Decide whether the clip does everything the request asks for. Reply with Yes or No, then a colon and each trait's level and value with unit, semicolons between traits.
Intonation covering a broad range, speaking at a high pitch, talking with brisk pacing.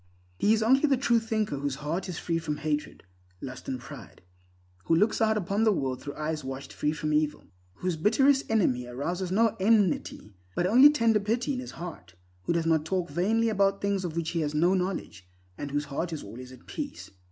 No: wide, 6.6 semitones; medium, 175 Hz; fast, 210 wpm